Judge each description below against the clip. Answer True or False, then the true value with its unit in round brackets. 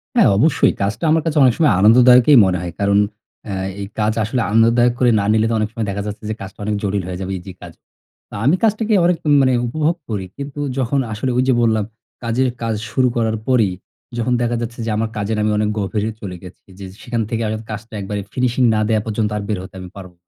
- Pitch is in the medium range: False (110 Hz)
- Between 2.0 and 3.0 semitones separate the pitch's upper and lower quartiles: False (3.6 semitones)